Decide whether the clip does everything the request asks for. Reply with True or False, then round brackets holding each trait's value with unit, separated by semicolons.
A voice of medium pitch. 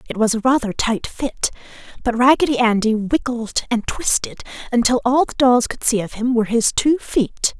False (240 Hz)